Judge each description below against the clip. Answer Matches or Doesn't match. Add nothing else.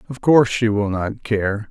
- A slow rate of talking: Doesn't match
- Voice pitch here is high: Doesn't match